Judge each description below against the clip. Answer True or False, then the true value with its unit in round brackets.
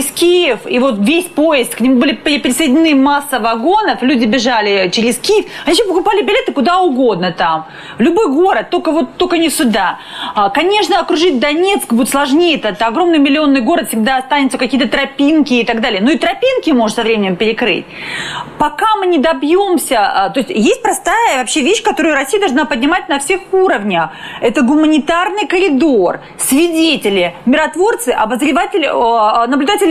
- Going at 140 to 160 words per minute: True (155 wpm)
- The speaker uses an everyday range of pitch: False (5.9 semitones)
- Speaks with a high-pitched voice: True (295 Hz)